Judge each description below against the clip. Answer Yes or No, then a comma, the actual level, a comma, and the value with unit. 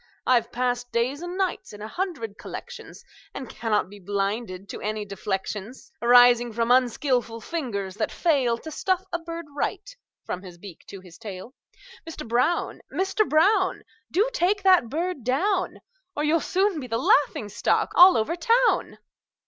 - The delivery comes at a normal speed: Yes, average, 160 wpm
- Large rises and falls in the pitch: Yes, wide, 8.2 semitones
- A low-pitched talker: No, very high, 250 Hz